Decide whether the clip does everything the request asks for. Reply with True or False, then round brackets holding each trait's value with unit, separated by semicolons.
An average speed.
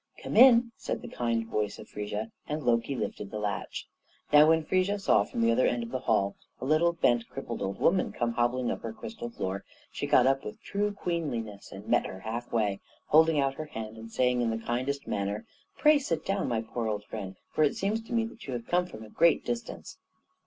False (225 wpm)